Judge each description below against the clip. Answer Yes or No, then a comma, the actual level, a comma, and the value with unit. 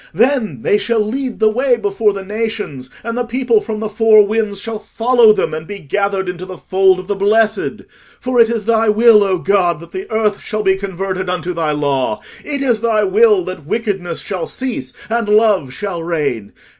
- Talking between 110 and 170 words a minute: No, average, 200 wpm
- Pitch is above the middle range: Yes, high, 210 Hz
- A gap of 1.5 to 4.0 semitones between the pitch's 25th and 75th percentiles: Yes, average, 3.6 semitones